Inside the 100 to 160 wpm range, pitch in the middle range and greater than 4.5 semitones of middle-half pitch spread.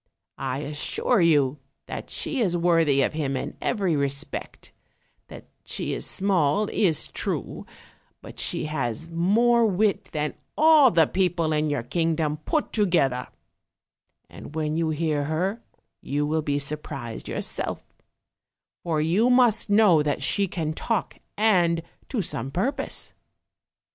Yes: average, 140 wpm; medium, 165 Hz; average, 5.1 semitones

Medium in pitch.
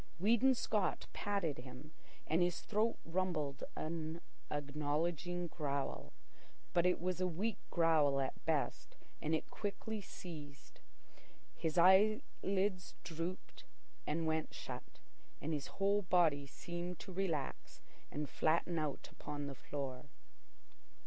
Yes: medium, 165 Hz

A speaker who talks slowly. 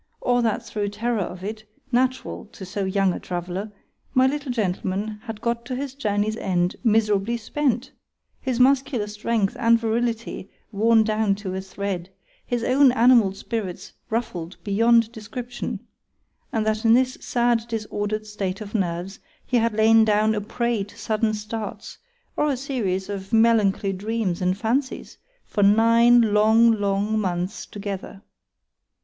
No: average, 145 wpm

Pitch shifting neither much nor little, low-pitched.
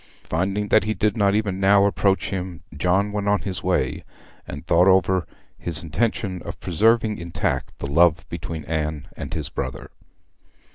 Yes: average, 3.6 semitones; very low, 95 Hz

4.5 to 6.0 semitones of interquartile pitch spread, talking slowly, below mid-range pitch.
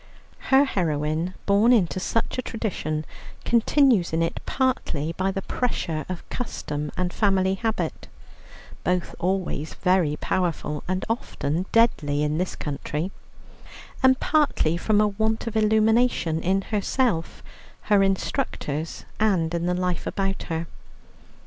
No: average, 5.1 semitones; slow, 130 wpm; medium, 185 Hz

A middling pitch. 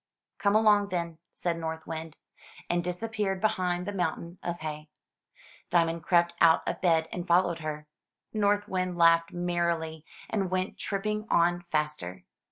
Yes: medium, 175 Hz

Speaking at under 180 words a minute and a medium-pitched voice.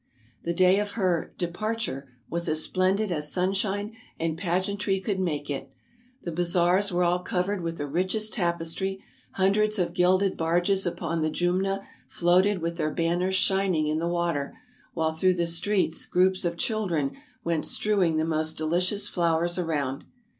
Yes: average, 160 wpm; medium, 175 Hz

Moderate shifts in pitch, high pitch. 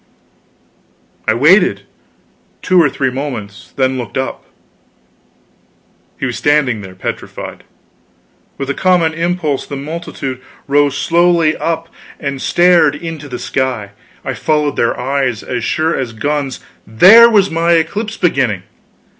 No: average, 4.6 semitones; medium, 145 Hz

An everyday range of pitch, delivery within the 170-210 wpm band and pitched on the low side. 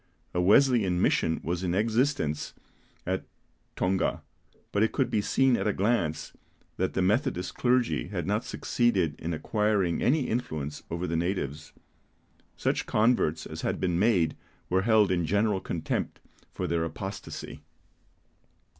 No: average, 4.8 semitones; average, 140 wpm; very low, 95 Hz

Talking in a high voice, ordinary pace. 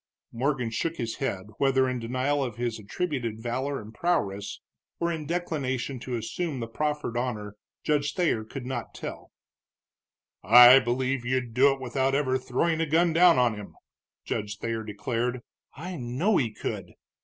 No: low, 130 Hz; average, 160 wpm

